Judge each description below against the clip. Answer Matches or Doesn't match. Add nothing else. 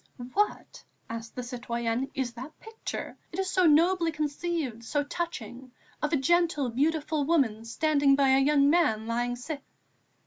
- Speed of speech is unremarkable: Matches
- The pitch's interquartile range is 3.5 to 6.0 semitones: Matches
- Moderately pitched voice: Doesn't match